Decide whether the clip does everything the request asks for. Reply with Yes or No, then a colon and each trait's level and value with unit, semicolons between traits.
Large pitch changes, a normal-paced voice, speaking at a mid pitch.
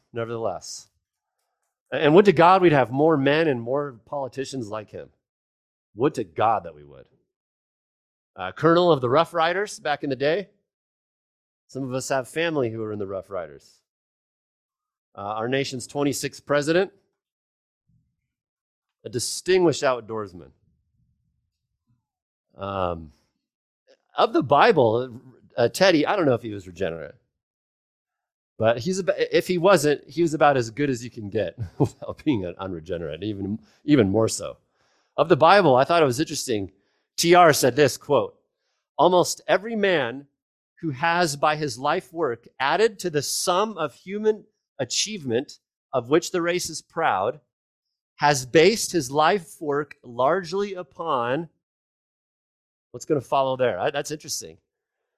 Yes: wide, 6.4 semitones; average, 145 wpm; medium, 145 Hz